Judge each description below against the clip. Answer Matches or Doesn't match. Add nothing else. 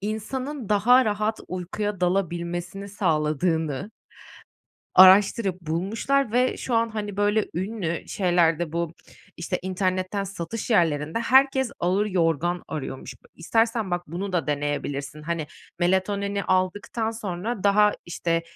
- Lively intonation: Doesn't match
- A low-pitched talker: Doesn't match